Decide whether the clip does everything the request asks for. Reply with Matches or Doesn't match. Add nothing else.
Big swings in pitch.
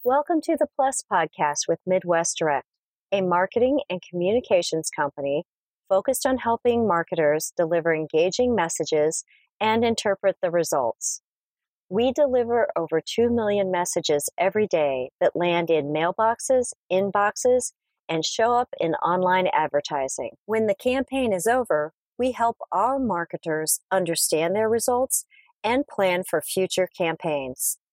Matches